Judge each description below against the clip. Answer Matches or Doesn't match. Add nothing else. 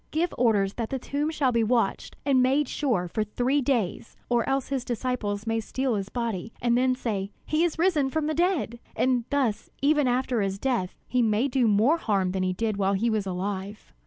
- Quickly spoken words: Matches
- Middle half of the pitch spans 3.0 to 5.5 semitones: Matches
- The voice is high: Matches